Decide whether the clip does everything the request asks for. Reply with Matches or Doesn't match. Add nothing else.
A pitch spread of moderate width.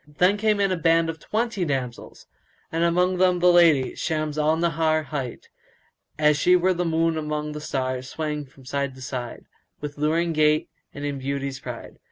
Matches